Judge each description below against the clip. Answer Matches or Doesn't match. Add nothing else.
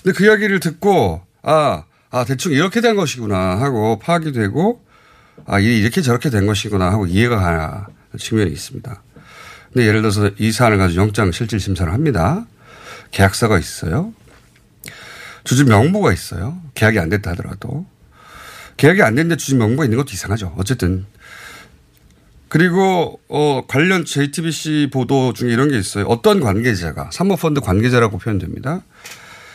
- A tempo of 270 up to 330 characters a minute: Doesn't match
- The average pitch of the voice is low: Matches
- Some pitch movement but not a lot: Doesn't match